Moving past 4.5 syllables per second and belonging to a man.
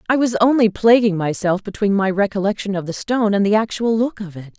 No: 6.0 syllables/s; female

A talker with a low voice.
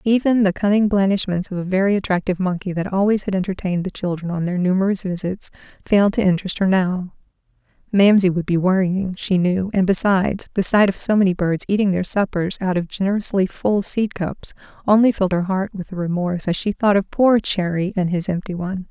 No: high, 190 Hz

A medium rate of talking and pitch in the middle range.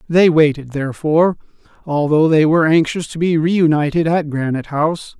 Yes: average, 150 wpm; medium, 155 Hz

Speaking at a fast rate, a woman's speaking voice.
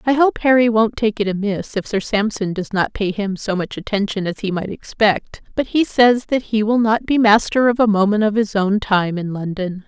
Yes: fast, 235 wpm; female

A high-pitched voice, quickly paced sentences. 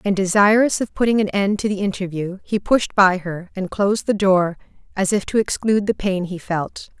Yes: high, 195 Hz; fast, 215 wpm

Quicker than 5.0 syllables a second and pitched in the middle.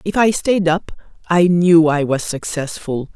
No: 4.0 syllables/s; medium, 170 Hz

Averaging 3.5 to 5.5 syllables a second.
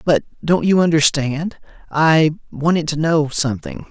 Yes: 4.5 syllables/s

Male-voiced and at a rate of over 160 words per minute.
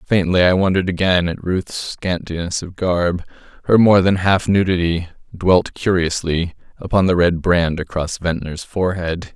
No: male; average, 150 wpm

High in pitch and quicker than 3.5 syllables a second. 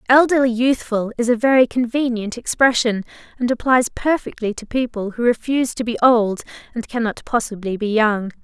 Yes: high, 235 Hz; 5.3 syllables/s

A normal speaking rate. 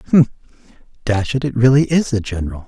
Yes: average, 180 wpm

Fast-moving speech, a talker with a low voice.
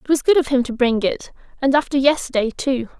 No: fast, 240 wpm; very high, 270 Hz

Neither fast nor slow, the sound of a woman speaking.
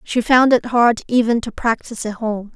No: fast, 210 wpm; female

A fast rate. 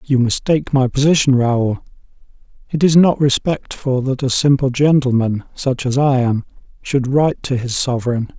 No: average, 155 wpm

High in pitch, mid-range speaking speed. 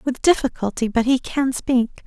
Yes: very high, 250 Hz; average, 175 wpm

